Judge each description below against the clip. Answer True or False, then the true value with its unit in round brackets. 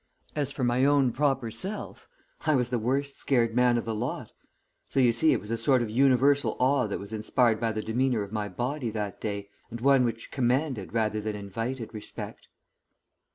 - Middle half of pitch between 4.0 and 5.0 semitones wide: False (3.5 semitones)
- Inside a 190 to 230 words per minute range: True (200 wpm)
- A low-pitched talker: True (120 Hz)